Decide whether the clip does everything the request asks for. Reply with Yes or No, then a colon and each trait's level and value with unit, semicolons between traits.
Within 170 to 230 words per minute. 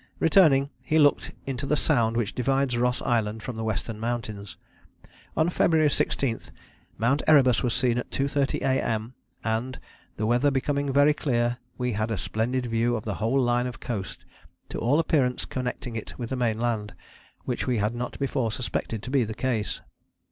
Yes: average, 175 wpm